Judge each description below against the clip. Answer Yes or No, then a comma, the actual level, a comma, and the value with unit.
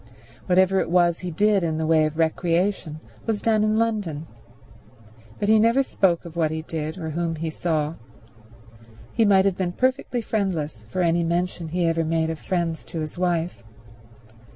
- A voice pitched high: No, medium, 170 Hz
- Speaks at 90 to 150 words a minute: No, average, 175 wpm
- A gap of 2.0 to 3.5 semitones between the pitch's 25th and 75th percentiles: Yes, average, 3.2 semitones